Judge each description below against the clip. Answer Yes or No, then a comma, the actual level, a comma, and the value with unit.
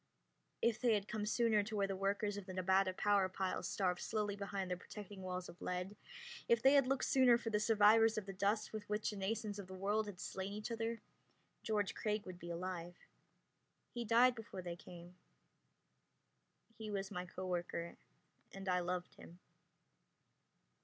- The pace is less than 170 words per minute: No, average, 180 wpm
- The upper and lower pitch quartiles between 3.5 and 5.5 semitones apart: No, average, 2.7 semitones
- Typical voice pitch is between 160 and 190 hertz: No, high, 200 Hz